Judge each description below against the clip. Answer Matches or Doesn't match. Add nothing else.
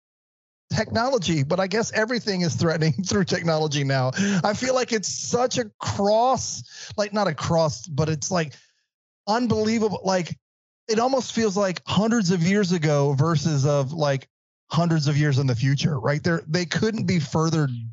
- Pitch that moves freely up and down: Matches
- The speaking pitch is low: Doesn't match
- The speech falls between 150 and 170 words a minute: Matches